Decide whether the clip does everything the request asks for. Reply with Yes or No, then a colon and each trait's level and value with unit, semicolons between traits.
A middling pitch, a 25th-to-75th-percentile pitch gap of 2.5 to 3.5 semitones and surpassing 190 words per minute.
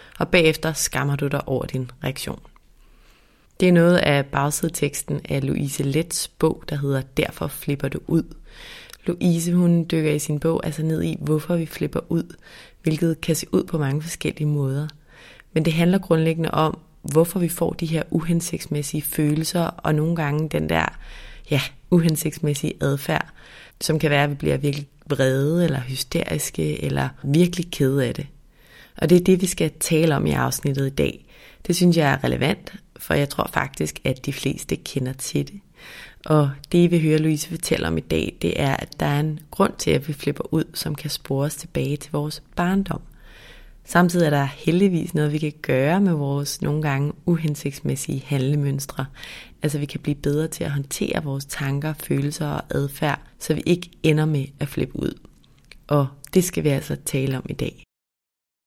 No: medium, 150 Hz; average, 2.8 semitones; average, 180 wpm